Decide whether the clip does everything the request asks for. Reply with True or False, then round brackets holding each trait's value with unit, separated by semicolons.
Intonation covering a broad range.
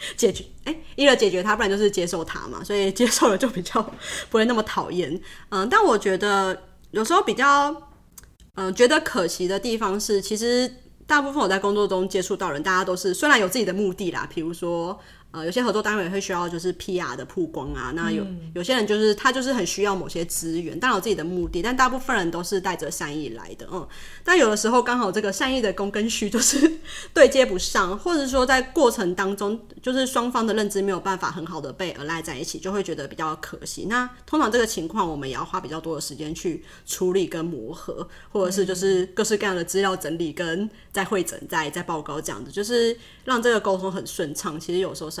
False (4.7 semitones)